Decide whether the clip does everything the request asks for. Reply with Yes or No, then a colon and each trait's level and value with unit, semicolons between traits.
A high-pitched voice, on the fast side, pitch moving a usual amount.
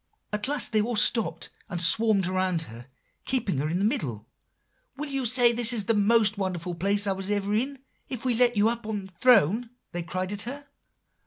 Yes: high, 210 Hz; fast, 215 wpm; average, 4.3 semitones